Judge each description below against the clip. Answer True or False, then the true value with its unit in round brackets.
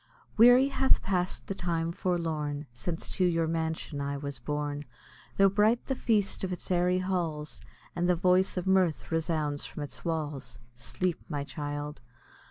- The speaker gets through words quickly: False (160 wpm)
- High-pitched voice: False (165 Hz)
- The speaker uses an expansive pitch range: False (3.9 semitones)